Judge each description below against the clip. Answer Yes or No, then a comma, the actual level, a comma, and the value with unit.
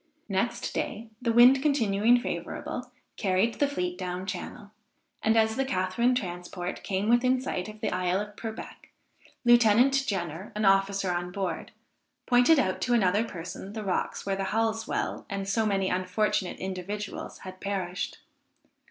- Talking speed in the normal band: Yes, average, 150 wpm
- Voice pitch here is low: No, high, 205 Hz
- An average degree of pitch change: Yes, average, 3.6 semitones